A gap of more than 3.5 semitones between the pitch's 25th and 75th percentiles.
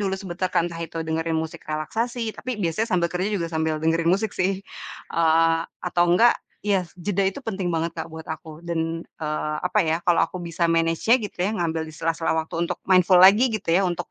No: average, 2.8 semitones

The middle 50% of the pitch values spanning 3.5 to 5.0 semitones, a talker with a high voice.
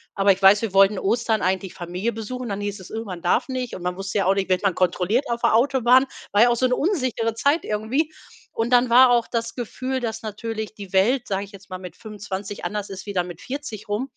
Yes: average, 3.9 semitones; high, 215 Hz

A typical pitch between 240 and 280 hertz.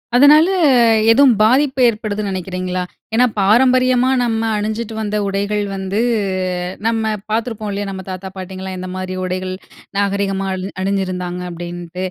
No: high, 200 Hz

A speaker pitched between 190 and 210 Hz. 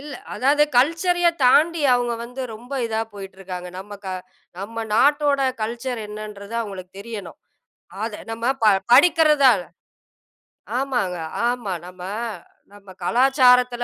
No: high, 240 Hz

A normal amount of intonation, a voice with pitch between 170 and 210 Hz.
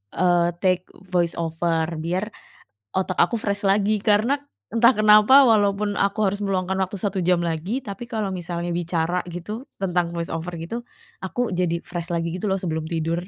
Yes: average, 3.5 semitones; medium, 185 Hz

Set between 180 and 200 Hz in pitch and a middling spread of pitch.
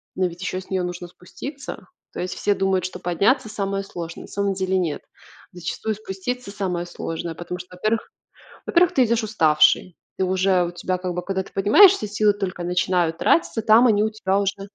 Yes: high, 190 Hz; average, 3.0 semitones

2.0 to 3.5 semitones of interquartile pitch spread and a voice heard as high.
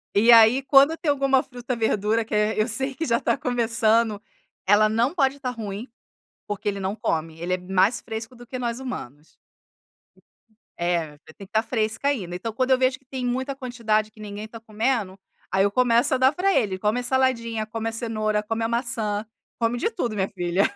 Yes: average, 3.2 semitones; high, 225 Hz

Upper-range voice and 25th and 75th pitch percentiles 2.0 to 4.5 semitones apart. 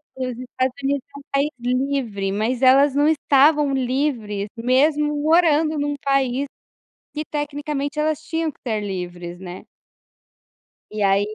Yes: very high, 275 Hz; average, 4.1 semitones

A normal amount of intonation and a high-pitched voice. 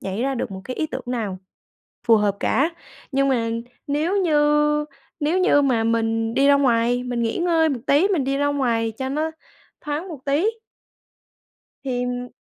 Yes: average, 4.2 semitones; very high, 270 Hz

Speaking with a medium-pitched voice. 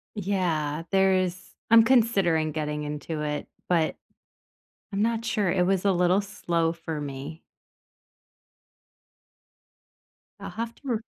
Yes: medium, 180 Hz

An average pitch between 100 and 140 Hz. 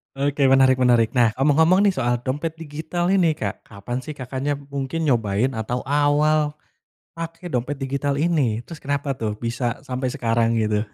Yes: low, 135 Hz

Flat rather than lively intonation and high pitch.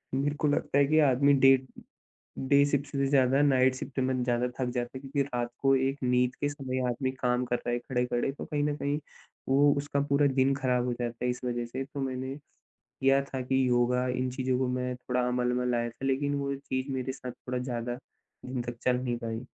No: narrow, 1.8 semitones; low, 130 Hz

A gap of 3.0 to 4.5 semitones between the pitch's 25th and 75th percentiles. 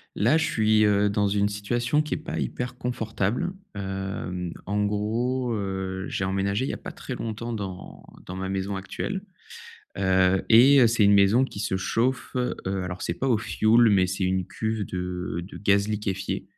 Yes: average, 3.4 semitones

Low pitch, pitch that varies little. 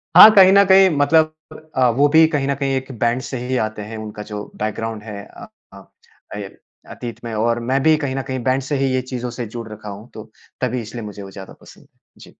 No: low, 125 Hz; average, 4.2 semitones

